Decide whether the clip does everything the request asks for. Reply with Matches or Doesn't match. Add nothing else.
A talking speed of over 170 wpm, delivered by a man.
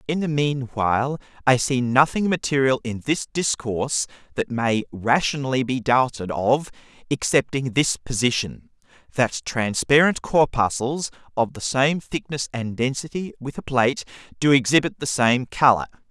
Doesn't match